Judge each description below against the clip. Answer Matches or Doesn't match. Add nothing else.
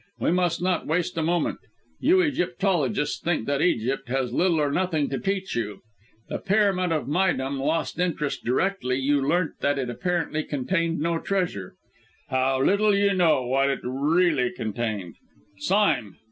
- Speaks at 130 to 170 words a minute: Matches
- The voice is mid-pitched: Matches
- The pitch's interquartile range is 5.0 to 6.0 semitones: Matches